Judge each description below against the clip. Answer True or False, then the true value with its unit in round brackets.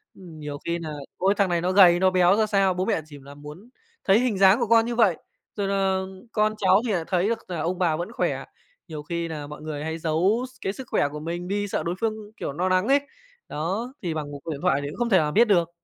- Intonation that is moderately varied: True (4.2 semitones)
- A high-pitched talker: False (180 Hz)